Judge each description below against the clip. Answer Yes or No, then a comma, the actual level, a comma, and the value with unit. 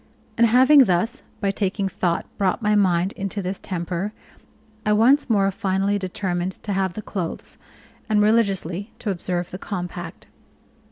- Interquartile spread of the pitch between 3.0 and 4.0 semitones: No, narrow, 2.6 semitones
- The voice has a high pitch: Yes, high, 195 Hz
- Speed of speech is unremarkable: Yes, average, 150 wpm